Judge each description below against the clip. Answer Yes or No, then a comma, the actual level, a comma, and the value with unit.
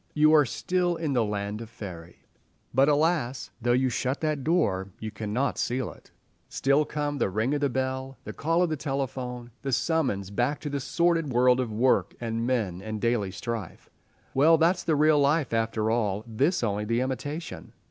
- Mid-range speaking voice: No, low, 130 Hz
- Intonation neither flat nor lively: Yes, average, 4.8 semitones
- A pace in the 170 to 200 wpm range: Yes, average, 180 wpm